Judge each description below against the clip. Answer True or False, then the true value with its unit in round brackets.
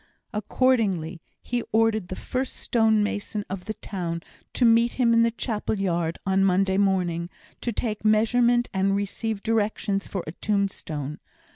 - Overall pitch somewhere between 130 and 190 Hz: False (205 Hz)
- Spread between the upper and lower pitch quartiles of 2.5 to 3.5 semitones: True (3.1 semitones)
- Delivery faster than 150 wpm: False (145 wpm)